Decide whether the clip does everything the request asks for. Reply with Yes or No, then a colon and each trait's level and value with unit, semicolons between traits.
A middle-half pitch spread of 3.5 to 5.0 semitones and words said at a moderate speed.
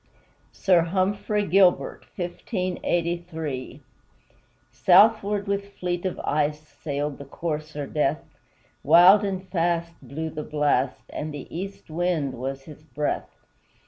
No: average, 4.1 semitones; slow, 110 wpm